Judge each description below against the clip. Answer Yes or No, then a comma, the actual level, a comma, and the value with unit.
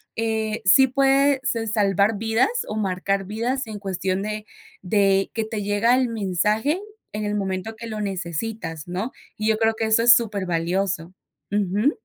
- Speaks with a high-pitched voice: Yes, high, 210 Hz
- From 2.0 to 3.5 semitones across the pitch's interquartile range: Yes, narrow, 2.6 semitones